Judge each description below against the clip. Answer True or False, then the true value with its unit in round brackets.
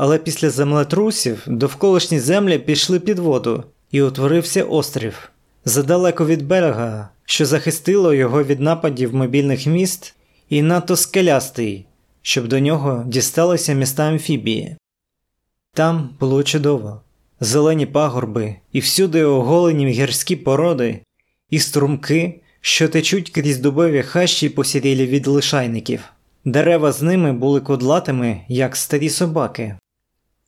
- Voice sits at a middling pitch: True (145 Hz)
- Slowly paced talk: False (115 wpm)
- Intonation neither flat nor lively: True (3.8 semitones)